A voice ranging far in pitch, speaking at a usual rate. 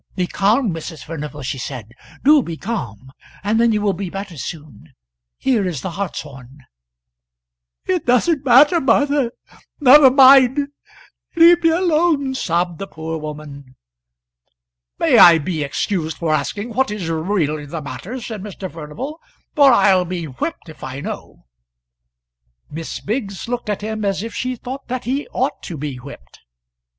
Yes: wide, 8.7 semitones; average, 155 wpm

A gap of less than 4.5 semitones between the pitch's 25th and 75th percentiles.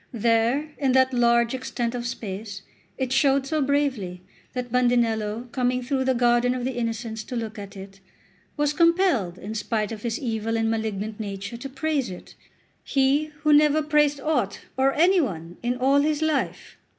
Yes: average, 3.9 semitones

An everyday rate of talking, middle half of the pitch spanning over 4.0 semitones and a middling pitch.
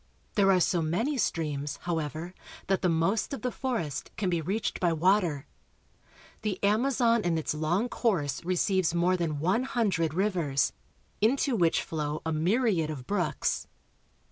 Yes: average, 150 wpm; average, 5.0 semitones; medium, 175 Hz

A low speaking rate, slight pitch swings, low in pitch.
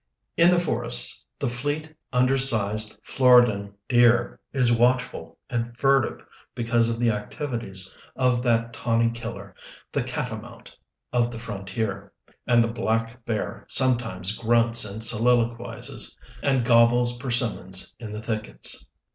Yes: slow, 125 wpm; narrow, 1.9 semitones; low, 115 Hz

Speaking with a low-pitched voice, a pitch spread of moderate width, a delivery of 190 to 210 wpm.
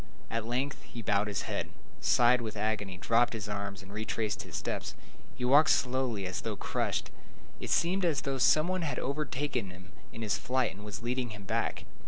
Yes: low, 115 Hz; average, 4.2 semitones; average, 200 wpm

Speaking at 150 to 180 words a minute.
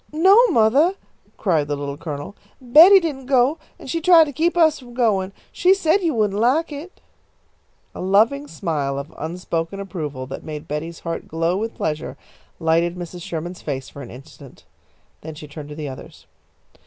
Yes: average, 175 wpm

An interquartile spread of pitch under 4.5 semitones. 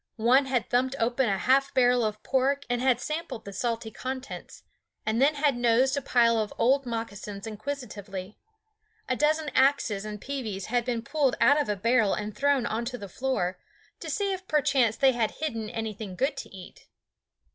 Yes: average, 4.0 semitones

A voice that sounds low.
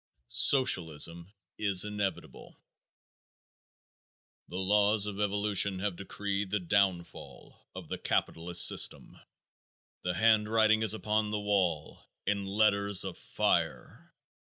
Yes: low, 100 Hz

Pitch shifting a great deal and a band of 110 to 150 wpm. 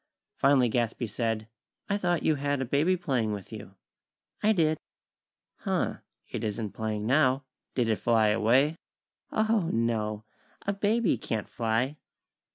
Yes: wide, 6.0 semitones; average, 140 wpm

